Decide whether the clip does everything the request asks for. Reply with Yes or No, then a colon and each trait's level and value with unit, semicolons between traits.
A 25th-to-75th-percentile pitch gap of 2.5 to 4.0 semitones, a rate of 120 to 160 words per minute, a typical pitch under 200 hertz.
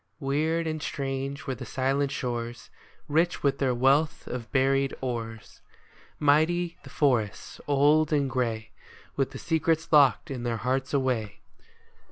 Yes: average, 3.1 semitones; average, 140 wpm; low, 135 Hz